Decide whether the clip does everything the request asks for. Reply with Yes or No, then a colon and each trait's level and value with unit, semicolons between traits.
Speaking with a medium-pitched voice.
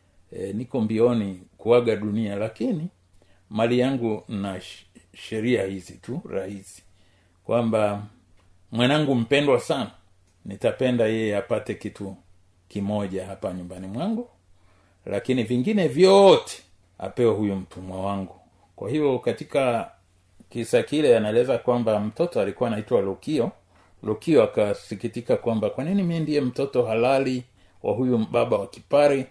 No: low, 105 Hz